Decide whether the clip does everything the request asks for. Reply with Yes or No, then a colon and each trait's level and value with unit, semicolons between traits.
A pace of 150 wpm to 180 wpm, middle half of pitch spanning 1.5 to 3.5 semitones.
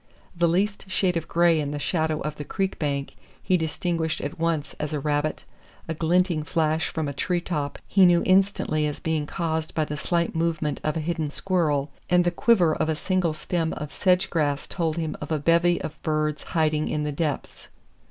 No: average, 200 wpm; narrow, 2.4 semitones